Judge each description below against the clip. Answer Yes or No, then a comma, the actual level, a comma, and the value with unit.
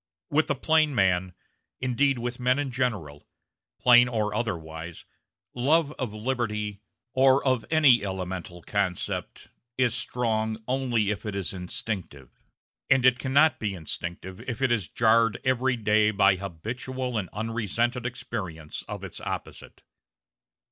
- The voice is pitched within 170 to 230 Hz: No, low, 115 Hz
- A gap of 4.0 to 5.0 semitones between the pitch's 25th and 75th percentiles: Yes, average, 4.5 semitones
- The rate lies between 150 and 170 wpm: No, slow, 135 wpm